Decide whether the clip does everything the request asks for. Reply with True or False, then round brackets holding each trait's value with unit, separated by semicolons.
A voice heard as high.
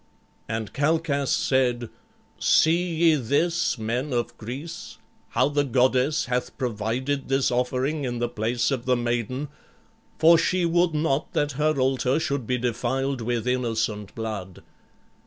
False (130 Hz)